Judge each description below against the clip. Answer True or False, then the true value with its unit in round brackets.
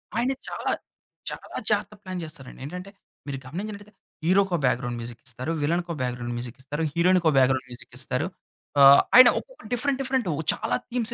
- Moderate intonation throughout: False (8.3 semitones)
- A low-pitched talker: False (170 Hz)